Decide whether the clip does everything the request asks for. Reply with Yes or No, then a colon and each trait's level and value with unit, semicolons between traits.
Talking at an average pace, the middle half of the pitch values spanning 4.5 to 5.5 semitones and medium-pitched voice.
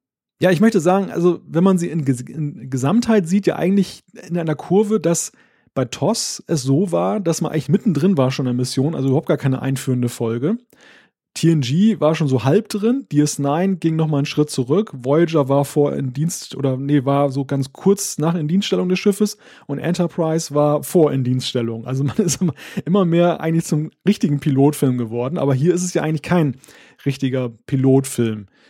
No: fast, 195 wpm; average, 5.2 semitones; medium, 155 Hz